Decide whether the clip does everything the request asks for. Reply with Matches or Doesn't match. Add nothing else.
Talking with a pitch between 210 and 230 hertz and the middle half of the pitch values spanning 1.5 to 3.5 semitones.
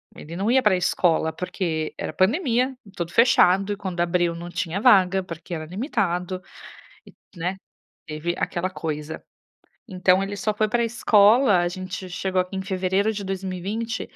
Doesn't match